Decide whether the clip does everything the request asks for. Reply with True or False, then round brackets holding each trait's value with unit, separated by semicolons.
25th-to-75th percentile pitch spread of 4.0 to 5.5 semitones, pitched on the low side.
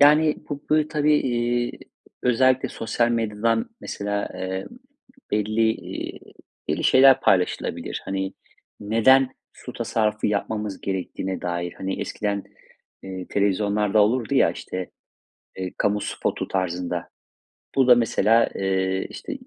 True (4.3 semitones; 105 Hz)